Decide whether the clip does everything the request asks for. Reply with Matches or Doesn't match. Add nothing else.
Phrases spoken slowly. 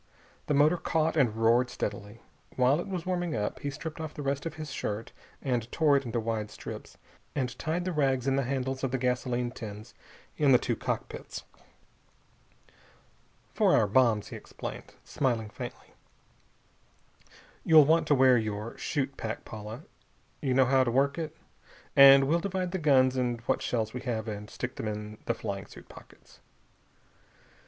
Doesn't match